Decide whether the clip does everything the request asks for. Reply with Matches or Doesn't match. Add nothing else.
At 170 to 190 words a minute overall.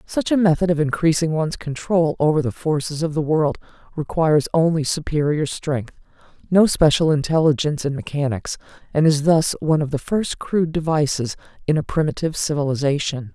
Doesn't match